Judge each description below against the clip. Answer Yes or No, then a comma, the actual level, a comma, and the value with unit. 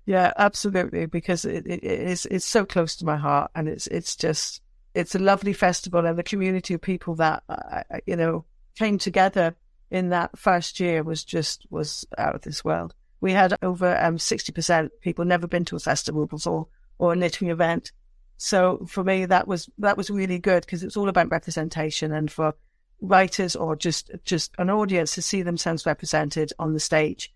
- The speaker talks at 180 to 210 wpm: Yes, average, 195 wpm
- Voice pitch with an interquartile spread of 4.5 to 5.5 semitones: No, average, 2.8 semitones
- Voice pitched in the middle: Yes, medium, 175 Hz